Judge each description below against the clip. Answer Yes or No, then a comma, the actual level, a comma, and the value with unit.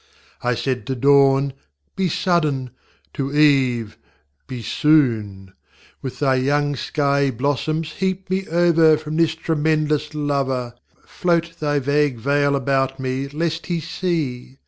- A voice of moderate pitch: Yes, medium, 145 Hz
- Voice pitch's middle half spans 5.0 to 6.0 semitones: No, average, 3.1 semitones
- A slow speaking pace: Yes, slow, 125 wpm